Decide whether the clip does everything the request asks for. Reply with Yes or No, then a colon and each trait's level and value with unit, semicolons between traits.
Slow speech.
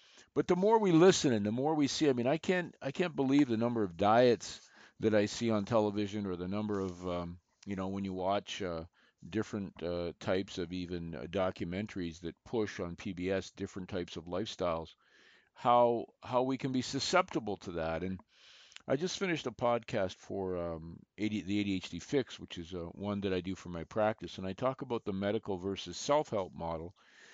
No: average, 200 wpm